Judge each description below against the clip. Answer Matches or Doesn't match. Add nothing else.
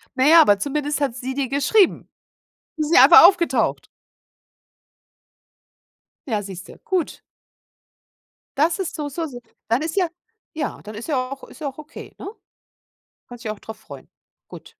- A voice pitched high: Matches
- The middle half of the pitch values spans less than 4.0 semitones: Doesn't match